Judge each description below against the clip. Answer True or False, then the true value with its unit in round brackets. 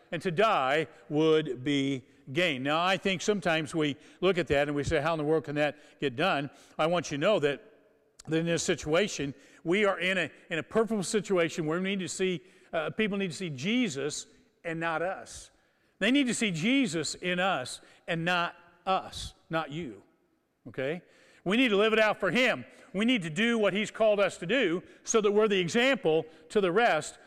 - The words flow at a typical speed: False (210 wpm)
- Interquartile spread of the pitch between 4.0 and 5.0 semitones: True (4.5 semitones)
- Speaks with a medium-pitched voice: True (175 Hz)